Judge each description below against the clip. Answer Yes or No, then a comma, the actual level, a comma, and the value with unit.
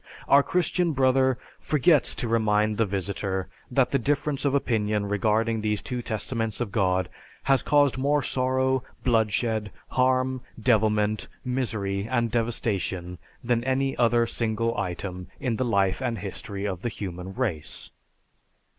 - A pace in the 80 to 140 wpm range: Yes, slow, 135 wpm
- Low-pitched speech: Yes, low, 115 Hz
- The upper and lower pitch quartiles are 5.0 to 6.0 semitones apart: No, average, 4.0 semitones